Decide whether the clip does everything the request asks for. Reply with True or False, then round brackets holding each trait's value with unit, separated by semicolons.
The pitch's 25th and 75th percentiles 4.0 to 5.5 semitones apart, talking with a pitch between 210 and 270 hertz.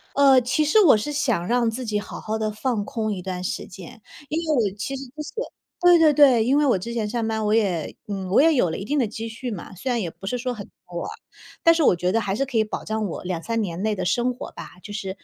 True (4.7 semitones; 220 Hz)